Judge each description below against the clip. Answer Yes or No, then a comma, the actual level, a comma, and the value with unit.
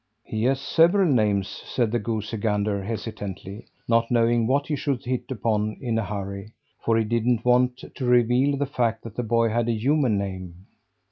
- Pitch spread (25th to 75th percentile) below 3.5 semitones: Yes, average, 2.7 semitones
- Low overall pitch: Yes, low, 115 Hz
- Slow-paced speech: No, average, 185 wpm